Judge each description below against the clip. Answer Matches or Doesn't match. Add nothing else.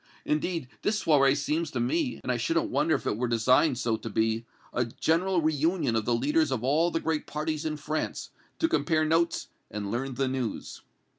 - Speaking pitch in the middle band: Matches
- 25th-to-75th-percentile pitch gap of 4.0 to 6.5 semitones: Matches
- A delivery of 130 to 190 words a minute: Doesn't match